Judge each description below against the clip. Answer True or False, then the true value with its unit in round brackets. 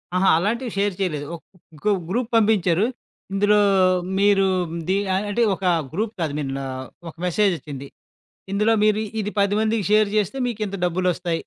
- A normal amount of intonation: True (3.1 semitones)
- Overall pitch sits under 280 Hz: True (200 Hz)